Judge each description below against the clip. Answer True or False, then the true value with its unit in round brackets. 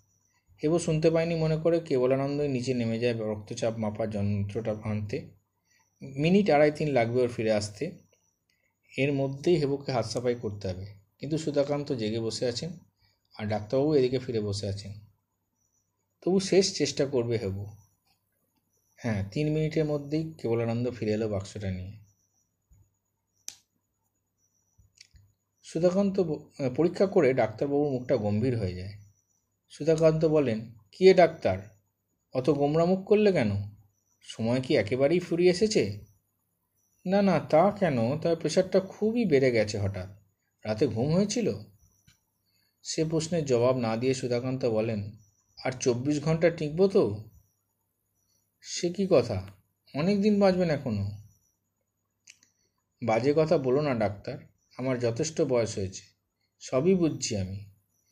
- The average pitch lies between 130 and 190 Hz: False (115 Hz)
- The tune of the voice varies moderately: False (6.8 semitones)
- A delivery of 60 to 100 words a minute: False (120 wpm)